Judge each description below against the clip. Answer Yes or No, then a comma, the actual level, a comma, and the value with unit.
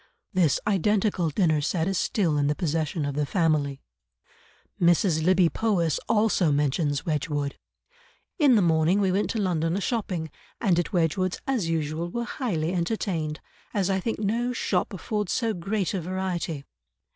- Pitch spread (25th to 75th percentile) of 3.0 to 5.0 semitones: Yes, average, 4.2 semitones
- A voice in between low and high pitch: Yes, medium, 175 Hz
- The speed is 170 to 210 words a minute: No, average, 155 wpm